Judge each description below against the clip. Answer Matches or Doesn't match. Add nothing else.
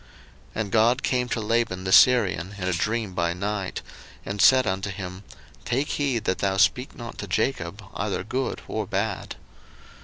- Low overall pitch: Matches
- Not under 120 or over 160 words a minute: Doesn't match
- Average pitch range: Matches